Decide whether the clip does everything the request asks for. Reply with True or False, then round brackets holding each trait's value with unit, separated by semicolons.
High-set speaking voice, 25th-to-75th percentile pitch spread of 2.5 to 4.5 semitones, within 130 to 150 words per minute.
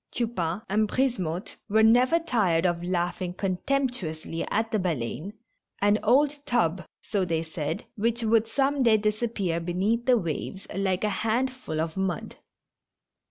False (205 Hz; 5.1 semitones; 145 wpm)